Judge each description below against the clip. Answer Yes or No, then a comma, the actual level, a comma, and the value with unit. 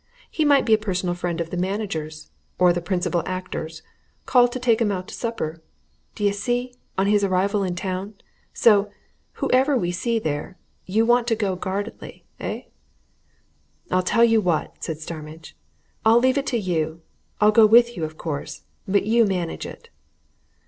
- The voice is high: Yes, high, 195 Hz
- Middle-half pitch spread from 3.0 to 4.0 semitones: No, average, 4.5 semitones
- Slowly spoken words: No, average, 170 wpm